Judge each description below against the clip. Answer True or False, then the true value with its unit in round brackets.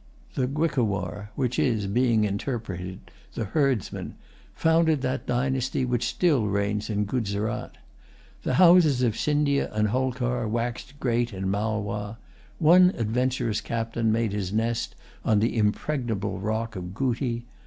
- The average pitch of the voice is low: True (115 Hz)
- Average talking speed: False (130 wpm)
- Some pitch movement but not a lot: True (3.8 semitones)